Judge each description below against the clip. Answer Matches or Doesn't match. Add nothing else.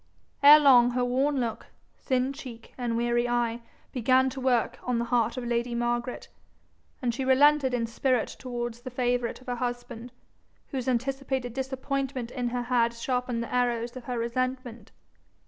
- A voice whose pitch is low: Doesn't match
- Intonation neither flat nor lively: Doesn't match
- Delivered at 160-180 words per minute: Matches